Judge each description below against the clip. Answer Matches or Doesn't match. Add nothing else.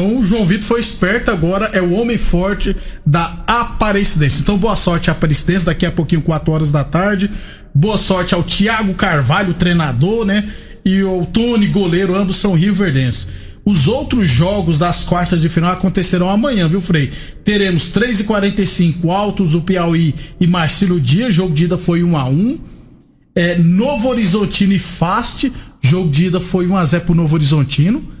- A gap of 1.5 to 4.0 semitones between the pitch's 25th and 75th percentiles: Matches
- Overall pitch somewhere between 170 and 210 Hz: Matches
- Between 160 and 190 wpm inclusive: Matches